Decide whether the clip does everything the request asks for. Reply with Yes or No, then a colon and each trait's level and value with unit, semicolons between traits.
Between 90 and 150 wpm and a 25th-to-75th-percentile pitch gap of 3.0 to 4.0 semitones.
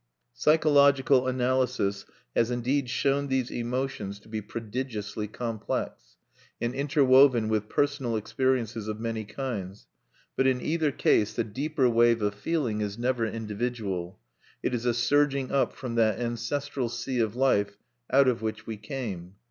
Yes: average, 145 wpm; average, 3.5 semitones